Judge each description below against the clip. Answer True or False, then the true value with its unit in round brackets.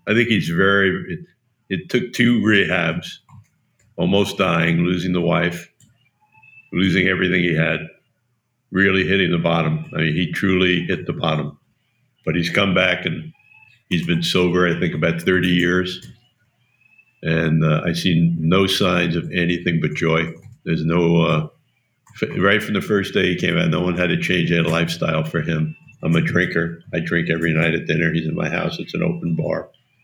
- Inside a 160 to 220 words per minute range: True (180 wpm)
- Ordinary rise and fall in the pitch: True (4.5 semitones)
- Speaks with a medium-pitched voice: False (90 Hz)